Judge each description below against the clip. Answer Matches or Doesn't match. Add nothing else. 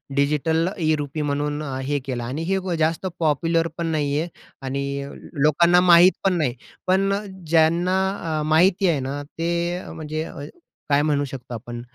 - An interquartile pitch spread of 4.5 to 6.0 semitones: Doesn't match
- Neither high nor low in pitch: Matches